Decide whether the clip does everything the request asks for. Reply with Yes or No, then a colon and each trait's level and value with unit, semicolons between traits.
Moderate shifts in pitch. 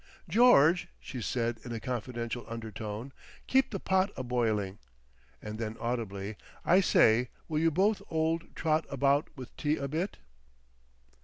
No: wide, 6.1 semitones